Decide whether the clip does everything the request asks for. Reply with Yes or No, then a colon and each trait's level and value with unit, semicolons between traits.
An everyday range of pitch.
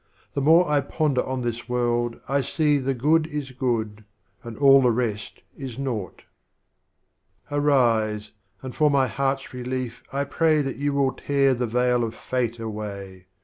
Yes: average, 3.2 semitones